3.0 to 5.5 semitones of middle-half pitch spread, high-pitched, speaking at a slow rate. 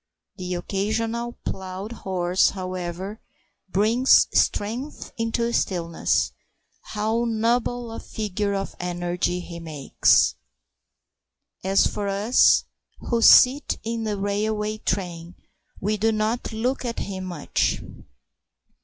Yes: average, 3.7 semitones; high, 210 Hz; slow, 110 wpm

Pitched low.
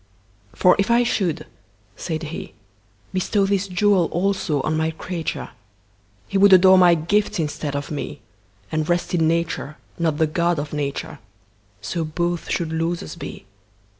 No: medium, 160 Hz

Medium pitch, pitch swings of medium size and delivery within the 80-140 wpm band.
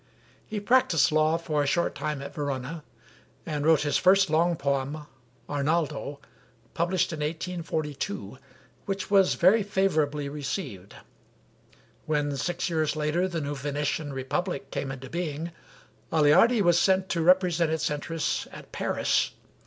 Yes: medium, 155 Hz; average, 3.3 semitones; slow, 135 wpm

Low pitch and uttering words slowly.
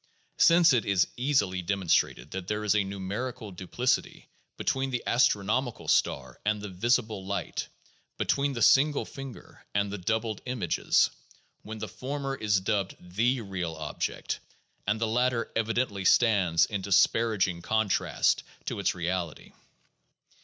Yes: low, 105 Hz; slow, 130 wpm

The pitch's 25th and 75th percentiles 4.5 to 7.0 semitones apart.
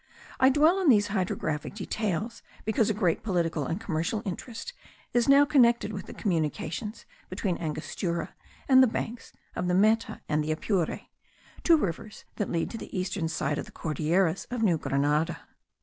Yes: wide, 5.6 semitones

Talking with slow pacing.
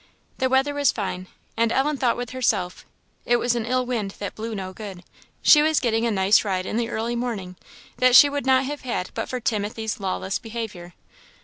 No: fast, 205 wpm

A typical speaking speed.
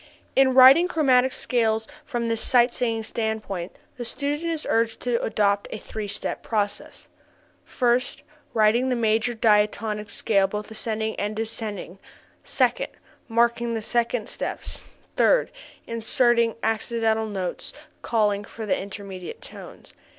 No: slow, 130 wpm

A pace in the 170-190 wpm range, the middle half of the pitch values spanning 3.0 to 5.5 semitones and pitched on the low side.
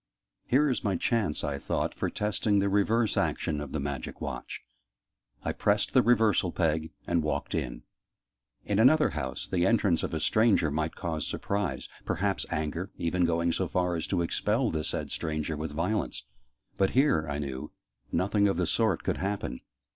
Yes: average, 175 wpm; average, 4.9 semitones; very low, 90 Hz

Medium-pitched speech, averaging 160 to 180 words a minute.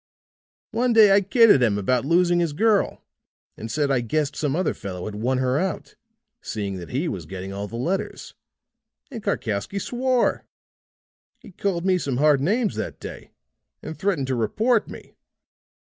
Yes: medium, 150 Hz; average, 165 wpm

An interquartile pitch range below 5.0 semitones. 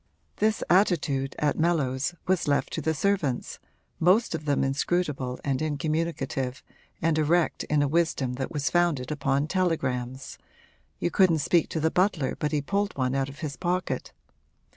Yes: average, 4.2 semitones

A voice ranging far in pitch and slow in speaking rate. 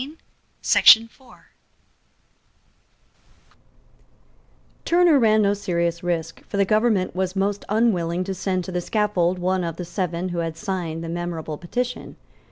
No: average, 3.1 semitones; slow, 125 wpm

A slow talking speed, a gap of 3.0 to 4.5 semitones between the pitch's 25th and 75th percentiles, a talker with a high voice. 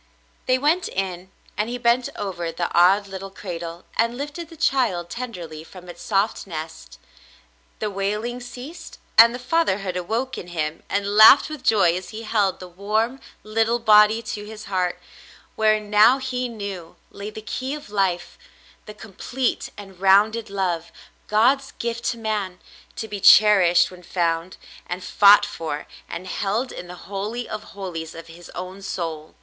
No: average, 165 wpm; average, 4.2 semitones; high, 205 Hz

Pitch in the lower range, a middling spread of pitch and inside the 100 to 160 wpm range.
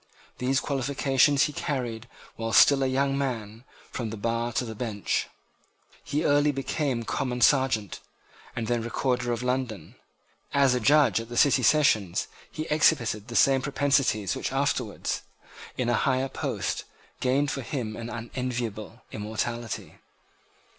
Yes: low, 125 Hz; average, 3.1 semitones; average, 140 wpm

